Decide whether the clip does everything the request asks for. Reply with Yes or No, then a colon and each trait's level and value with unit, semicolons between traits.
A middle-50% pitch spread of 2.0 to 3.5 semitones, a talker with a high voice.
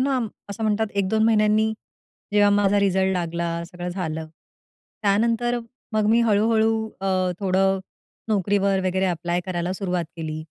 Yes: average, 3.1 semitones; high, 195 Hz